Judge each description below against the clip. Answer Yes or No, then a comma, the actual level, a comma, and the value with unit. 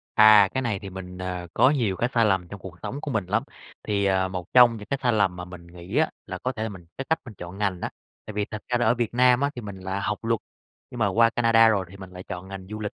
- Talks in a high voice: No, low, 105 Hz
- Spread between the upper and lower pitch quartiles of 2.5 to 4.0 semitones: Yes, average, 3.7 semitones